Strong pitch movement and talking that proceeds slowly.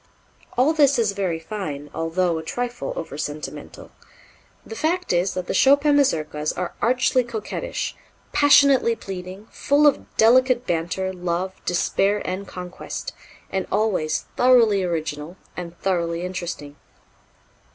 Yes: wide, 6.5 semitones; slow, 125 wpm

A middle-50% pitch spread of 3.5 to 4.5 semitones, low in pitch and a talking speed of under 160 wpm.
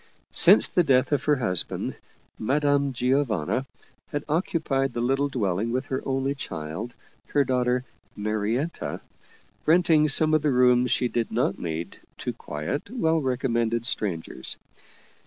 Yes: average, 3.8 semitones; low, 130 Hz; average, 140 wpm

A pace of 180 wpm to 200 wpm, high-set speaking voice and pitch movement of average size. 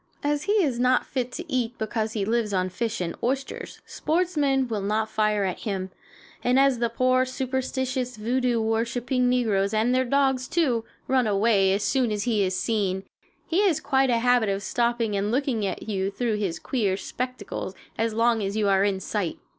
Yes: average, 190 wpm; high, 235 Hz; average, 3.8 semitones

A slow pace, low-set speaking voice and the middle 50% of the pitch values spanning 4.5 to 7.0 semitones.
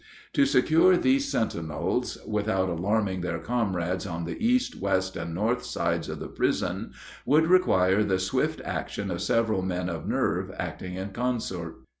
No: average, 155 wpm; very low, 95 Hz; average, 4.9 semitones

